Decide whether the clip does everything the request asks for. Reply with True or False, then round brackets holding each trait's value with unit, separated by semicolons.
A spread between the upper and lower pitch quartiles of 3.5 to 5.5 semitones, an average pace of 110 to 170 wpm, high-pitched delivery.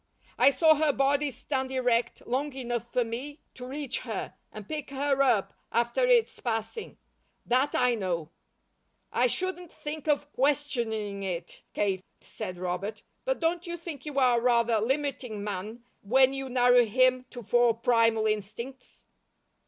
True (4.1 semitones; 150 wpm; 250 Hz)